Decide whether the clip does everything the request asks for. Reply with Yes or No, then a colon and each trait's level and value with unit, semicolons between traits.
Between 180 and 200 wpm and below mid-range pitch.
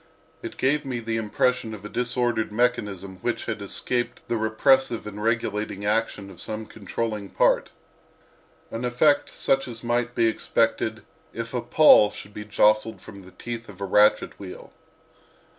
No: average, 155 wpm; low, 115 Hz